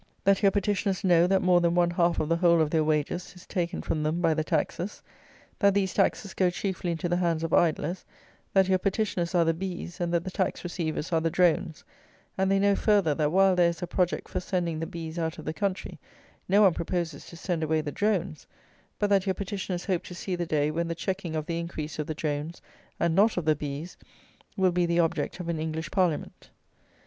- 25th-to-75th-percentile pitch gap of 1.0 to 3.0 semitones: Yes, average, 2.7 semitones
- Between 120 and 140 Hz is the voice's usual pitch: No, medium, 175 Hz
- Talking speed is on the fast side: Yes, fast, 230 wpm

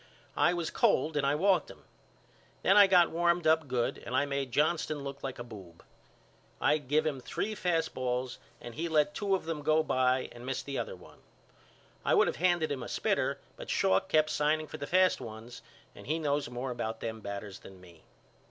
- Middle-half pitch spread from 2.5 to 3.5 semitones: No, average, 4.6 semitones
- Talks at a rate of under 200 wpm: No, fast, 205 wpm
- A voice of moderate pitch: Yes, medium, 145 Hz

